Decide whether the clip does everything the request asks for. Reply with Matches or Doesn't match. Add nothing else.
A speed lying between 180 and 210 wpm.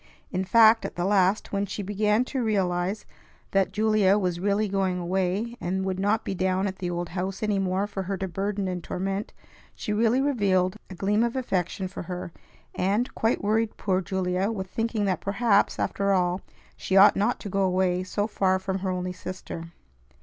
Matches